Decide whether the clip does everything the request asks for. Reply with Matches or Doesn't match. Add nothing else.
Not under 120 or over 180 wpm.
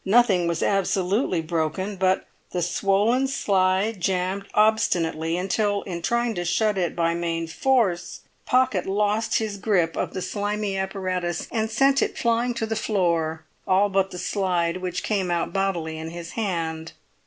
Matches